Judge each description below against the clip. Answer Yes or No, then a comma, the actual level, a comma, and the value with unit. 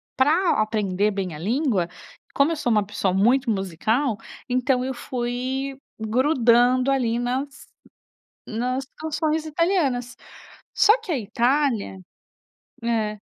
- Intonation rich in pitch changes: No, average, 4.2 semitones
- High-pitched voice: Yes, very high, 250 Hz